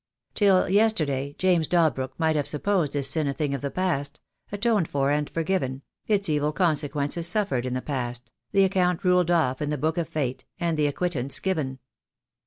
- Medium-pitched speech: Yes, medium, 155 Hz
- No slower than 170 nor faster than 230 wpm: Yes, average, 190 wpm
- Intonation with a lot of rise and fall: No, average, 4.4 semitones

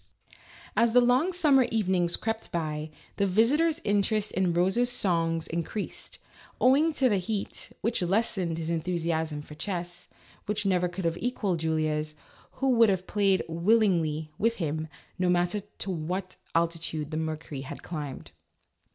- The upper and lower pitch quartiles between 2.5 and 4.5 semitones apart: No, average, 5.0 semitones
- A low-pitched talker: No, medium, 180 Hz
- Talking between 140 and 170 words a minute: Yes, average, 150 wpm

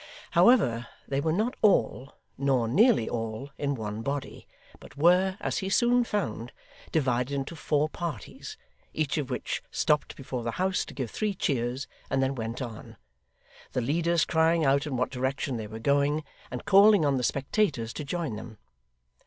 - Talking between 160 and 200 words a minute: Yes, average, 170 wpm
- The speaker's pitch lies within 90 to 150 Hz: Yes, medium, 140 Hz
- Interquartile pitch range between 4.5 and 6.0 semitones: Yes, wide, 5.5 semitones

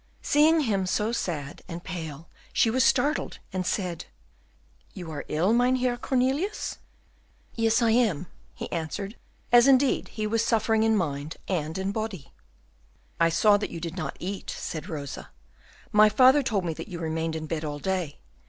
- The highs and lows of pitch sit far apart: Yes, wide, 6.2 semitones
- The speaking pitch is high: Yes, high, 195 Hz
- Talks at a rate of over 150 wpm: Yes, average, 165 wpm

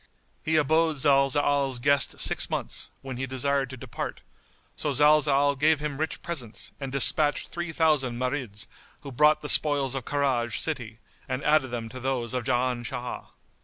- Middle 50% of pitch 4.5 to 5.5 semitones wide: No, average, 2.8 semitones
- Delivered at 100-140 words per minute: No, average, 165 wpm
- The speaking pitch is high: No, low, 135 Hz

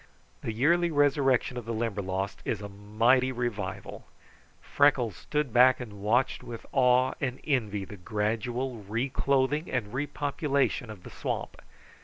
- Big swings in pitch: No, average, 4.1 semitones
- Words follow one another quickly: No, slow, 135 wpm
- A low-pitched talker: Yes, low, 125 Hz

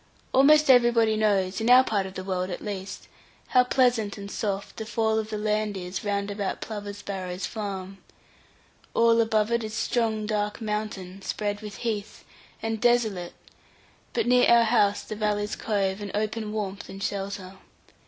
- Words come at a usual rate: Yes, average, 165 wpm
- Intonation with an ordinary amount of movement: No, narrow, 2.1 semitones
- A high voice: Yes, high, 210 Hz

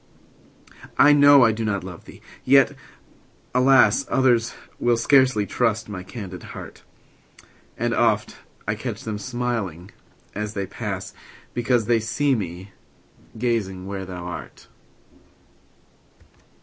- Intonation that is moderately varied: Yes, average, 3.8 semitones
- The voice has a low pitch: Yes, low, 110 Hz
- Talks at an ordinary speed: No, slow, 120 wpm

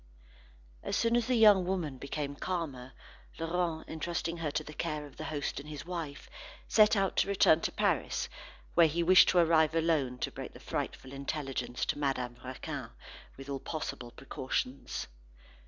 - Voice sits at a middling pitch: Yes, medium, 155 Hz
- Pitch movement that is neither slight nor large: Yes, average, 3.9 semitones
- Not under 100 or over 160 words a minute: No, average, 170 wpm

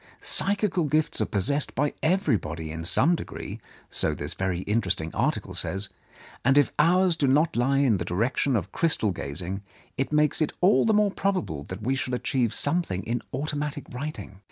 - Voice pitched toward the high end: No, low, 135 Hz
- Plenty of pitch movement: Yes, wide, 8.3 semitones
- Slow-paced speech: No, average, 175 wpm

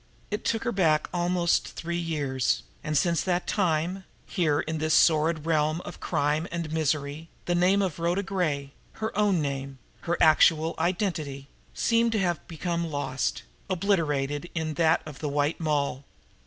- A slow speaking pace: No, average, 155 wpm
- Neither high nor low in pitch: Yes, medium, 160 Hz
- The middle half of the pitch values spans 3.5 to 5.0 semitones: No, average, 3.0 semitones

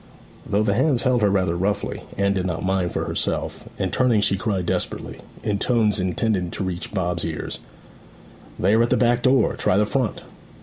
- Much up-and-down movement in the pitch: No, average, 3.9 semitones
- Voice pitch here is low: Yes, low, 100 Hz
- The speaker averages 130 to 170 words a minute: No, average, 190 wpm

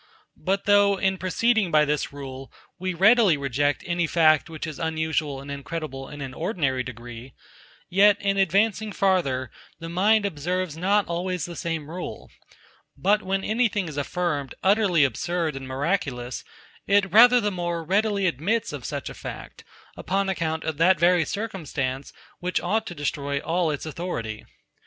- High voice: No, medium, 170 Hz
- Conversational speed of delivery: Yes, average, 155 wpm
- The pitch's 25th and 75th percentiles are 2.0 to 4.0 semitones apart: No, average, 5.2 semitones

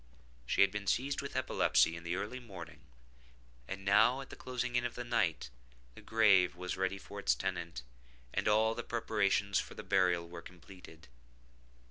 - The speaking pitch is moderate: No, low, 100 Hz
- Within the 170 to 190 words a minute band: Yes, average, 175 wpm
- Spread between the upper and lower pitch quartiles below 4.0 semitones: No, average, 4.7 semitones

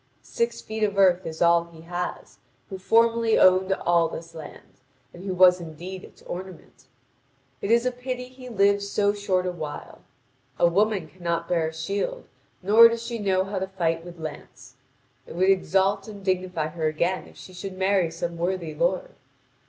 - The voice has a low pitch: No, medium, 185 Hz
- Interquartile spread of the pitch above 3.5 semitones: No, average, 3.0 semitones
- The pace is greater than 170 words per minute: Yes, average, 180 wpm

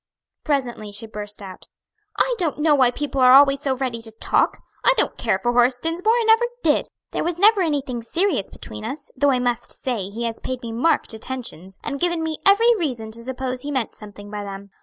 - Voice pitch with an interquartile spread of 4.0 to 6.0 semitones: Yes, wide, 5.4 semitones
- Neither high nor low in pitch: No, very high, 255 Hz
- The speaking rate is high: Yes, fast, 215 wpm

